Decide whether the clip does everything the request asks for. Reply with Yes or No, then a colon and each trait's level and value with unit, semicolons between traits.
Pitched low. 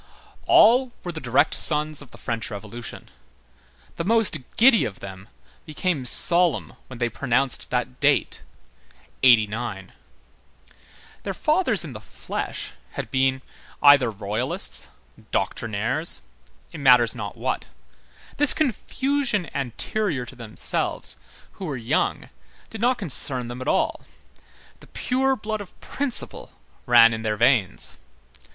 Yes: low, 130 Hz